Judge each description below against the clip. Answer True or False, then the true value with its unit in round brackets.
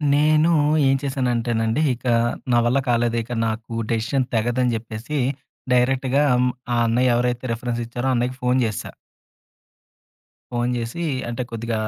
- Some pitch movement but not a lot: False (1.8 semitones)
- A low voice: True (120 Hz)